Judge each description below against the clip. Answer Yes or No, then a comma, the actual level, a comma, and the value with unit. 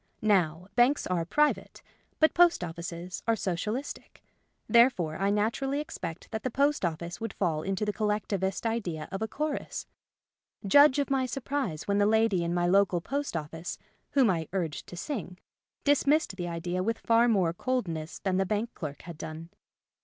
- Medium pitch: No, high, 195 Hz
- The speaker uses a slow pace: No, average, 175 wpm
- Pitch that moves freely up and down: Yes, wide, 5.9 semitones